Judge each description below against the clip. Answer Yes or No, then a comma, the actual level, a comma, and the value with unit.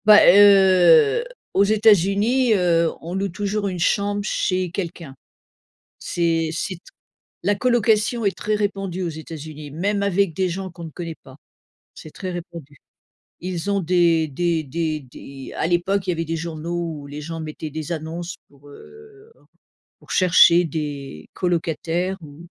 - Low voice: No, medium, 175 Hz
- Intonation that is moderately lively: Yes, average, 3.7 semitones